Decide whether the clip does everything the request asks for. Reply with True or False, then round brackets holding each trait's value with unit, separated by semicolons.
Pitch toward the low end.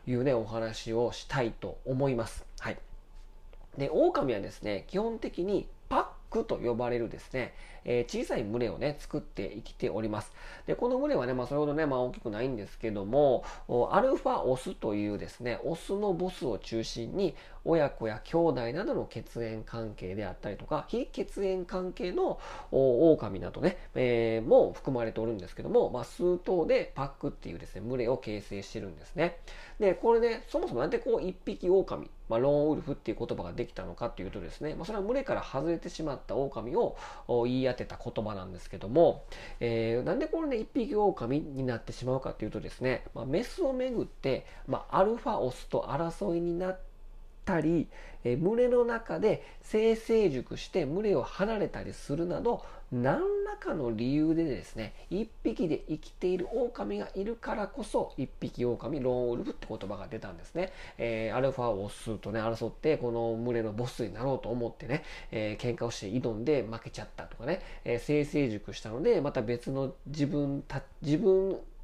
True (130 Hz)